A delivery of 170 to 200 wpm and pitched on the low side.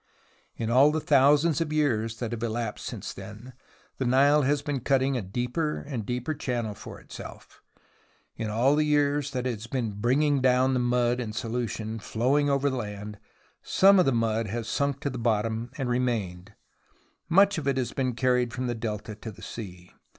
Yes: average, 190 wpm; low, 125 Hz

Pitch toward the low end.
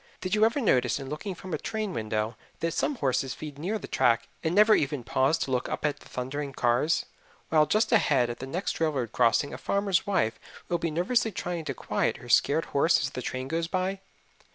No: medium, 155 Hz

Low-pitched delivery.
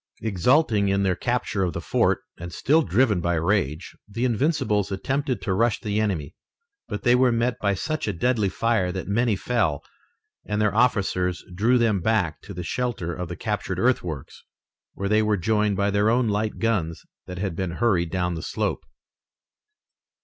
Yes: low, 105 Hz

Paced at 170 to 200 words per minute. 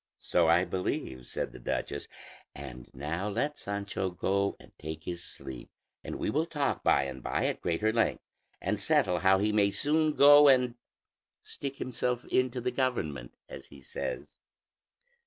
No: average, 160 wpm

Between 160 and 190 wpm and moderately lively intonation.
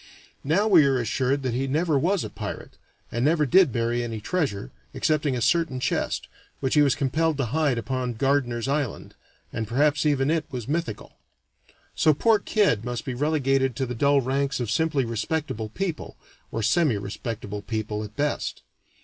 Yes: average, 170 wpm; average, 4.4 semitones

